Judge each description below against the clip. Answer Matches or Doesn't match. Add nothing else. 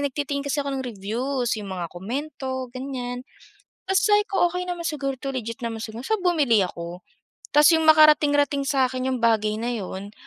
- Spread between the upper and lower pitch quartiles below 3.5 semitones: Doesn't match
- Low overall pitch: Doesn't match